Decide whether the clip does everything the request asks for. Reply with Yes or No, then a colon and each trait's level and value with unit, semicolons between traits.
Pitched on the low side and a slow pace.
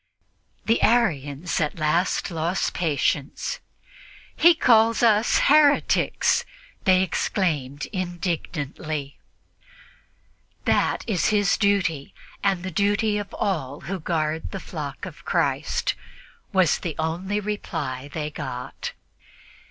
No: medium, 175 Hz; slow, 105 wpm